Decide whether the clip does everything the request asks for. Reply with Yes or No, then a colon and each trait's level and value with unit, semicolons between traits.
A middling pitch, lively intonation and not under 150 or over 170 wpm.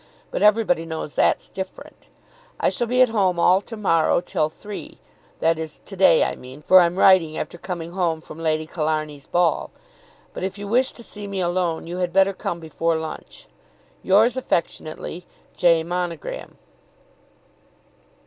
No: medium, 175 Hz; average, 3.2 semitones; average, 160 wpm